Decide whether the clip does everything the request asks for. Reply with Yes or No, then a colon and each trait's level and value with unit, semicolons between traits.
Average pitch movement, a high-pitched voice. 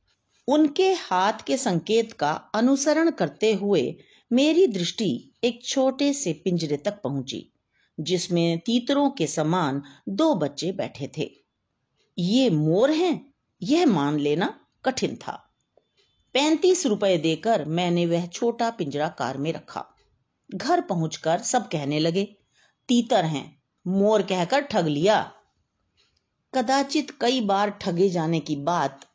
No: wide, 8.1 semitones; high, 200 Hz